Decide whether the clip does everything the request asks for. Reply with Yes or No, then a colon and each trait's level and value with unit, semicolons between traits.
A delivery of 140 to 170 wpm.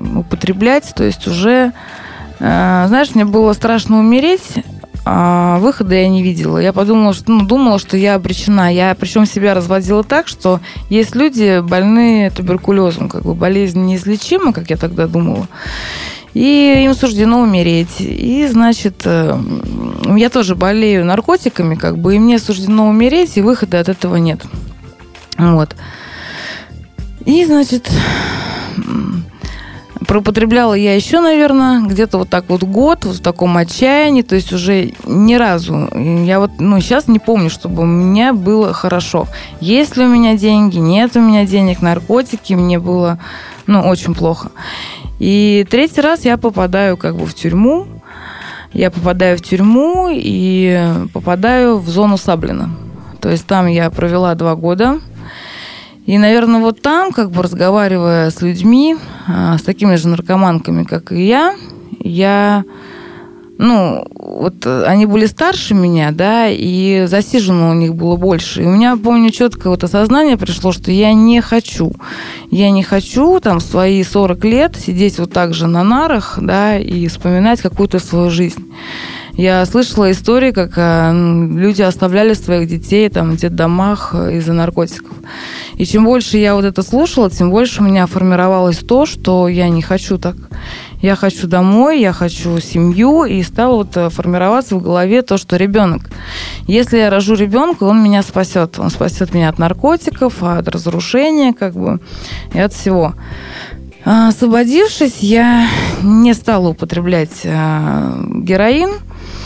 Yes: average, 145 wpm